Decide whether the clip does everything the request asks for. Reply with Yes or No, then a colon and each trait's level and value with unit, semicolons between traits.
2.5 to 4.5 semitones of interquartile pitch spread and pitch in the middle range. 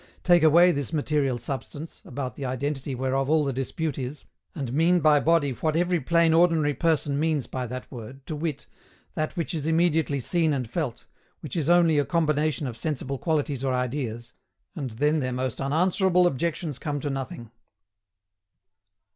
Yes: average, 3.6 semitones; medium, 145 Hz